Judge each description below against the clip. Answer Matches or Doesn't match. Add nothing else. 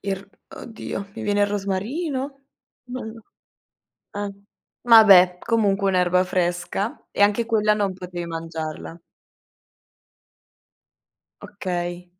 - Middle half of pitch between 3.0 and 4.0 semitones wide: Matches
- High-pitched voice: Matches